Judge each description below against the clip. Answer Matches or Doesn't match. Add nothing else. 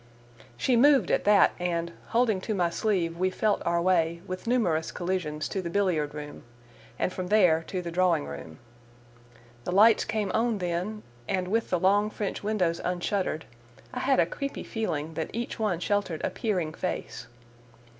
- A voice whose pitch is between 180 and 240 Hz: Matches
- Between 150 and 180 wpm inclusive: Matches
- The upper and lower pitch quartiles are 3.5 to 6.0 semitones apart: Matches